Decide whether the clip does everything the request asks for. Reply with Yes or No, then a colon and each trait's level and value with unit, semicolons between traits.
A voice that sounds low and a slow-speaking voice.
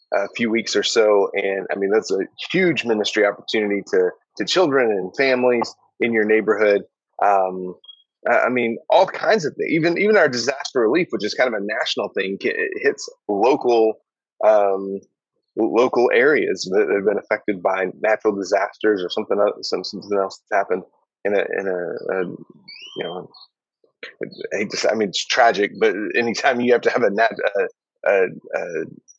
No: low, 125 Hz; average, 175 wpm